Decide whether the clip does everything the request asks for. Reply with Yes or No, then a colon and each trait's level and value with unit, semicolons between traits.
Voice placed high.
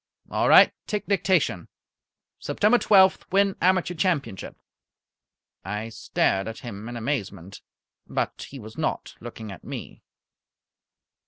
No: low, 120 Hz